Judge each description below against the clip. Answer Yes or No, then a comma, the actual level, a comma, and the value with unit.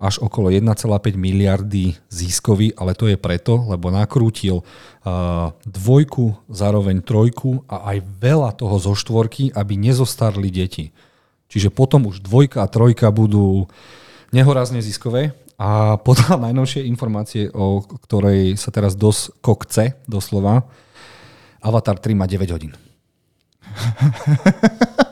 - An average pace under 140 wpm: Yes, average, 115 wpm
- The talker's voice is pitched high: No, low, 110 Hz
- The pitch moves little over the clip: No, average, 4.0 semitones